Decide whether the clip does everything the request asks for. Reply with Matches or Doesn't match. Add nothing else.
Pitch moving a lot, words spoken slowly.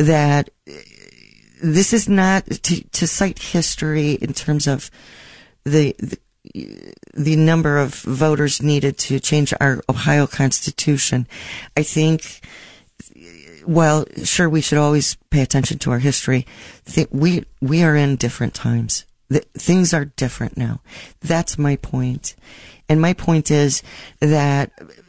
Doesn't match